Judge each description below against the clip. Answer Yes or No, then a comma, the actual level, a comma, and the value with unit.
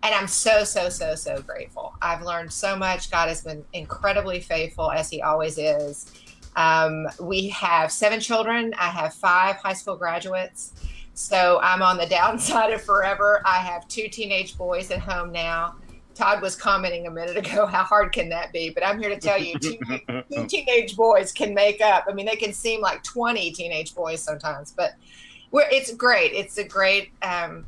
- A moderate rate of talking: Yes, average, 190 wpm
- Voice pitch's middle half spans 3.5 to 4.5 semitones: Yes, average, 3.8 semitones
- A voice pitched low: No, medium, 185 Hz